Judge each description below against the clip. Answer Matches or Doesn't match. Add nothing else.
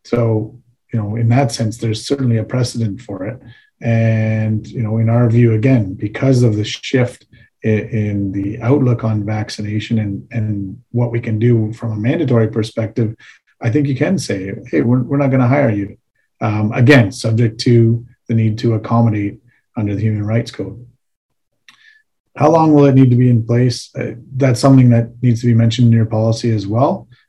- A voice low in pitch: Matches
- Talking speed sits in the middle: Matches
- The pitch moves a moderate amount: Doesn't match